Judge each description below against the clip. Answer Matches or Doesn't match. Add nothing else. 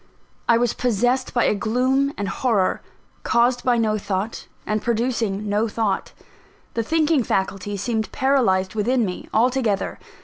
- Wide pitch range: Doesn't match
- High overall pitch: Matches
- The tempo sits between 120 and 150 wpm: Matches